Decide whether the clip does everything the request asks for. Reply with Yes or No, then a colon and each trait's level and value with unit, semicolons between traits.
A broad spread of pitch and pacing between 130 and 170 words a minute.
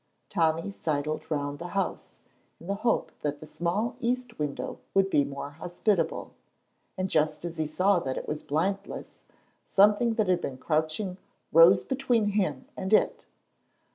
No: average, 4.8 semitones; average, 155 wpm